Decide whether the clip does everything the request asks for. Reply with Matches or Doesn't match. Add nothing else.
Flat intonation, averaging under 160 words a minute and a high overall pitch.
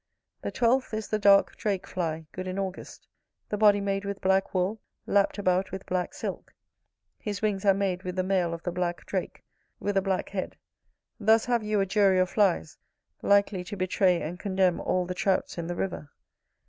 Doesn't match